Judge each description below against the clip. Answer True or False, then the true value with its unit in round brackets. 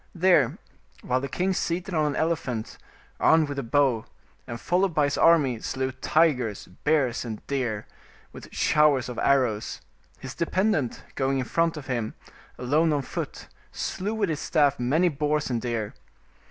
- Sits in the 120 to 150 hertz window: True (140 Hz)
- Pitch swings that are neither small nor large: True (4.5 semitones)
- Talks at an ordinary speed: True (160 wpm)